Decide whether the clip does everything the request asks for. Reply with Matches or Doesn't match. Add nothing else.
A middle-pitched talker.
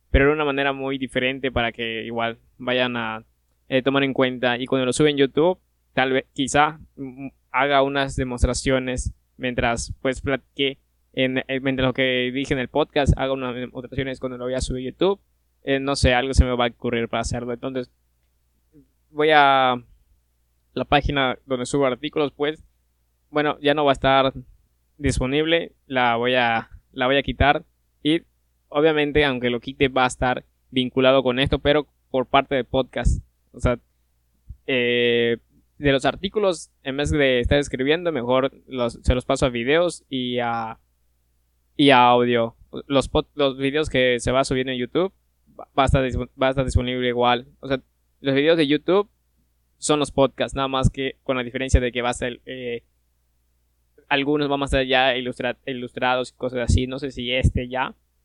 Doesn't match